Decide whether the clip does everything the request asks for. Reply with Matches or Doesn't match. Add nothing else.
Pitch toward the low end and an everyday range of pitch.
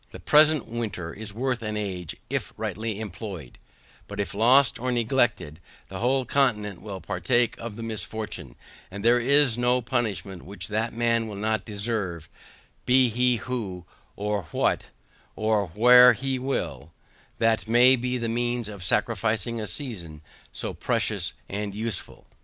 Matches